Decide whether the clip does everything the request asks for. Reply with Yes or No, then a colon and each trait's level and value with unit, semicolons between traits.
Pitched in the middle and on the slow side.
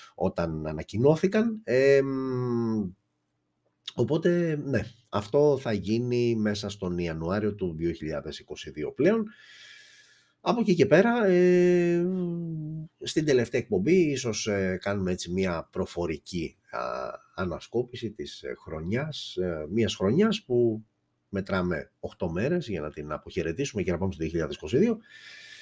No: low, 120 Hz; slow, 110 wpm